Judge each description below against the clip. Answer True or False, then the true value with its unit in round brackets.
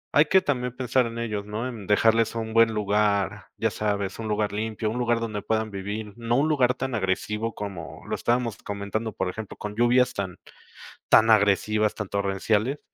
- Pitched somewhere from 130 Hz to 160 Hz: False (110 Hz)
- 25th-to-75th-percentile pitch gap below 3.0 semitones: True (2.4 semitones)